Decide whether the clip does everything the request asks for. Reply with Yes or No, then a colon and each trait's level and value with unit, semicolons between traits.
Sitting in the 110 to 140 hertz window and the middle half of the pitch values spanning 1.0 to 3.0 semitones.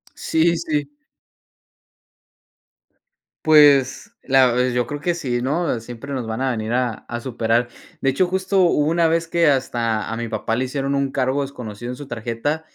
No: low, 135 Hz; average, 4.2 semitones